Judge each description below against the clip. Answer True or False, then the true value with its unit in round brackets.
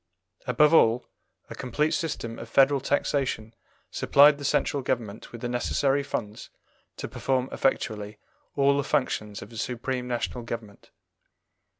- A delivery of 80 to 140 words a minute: True (135 wpm)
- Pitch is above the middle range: False (125 Hz)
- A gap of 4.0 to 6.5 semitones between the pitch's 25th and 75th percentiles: False (3.5 semitones)